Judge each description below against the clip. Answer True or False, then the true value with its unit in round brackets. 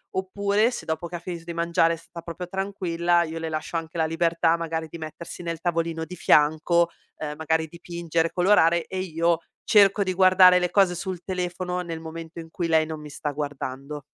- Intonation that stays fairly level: True (1.9 semitones)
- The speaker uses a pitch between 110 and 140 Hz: False (170 Hz)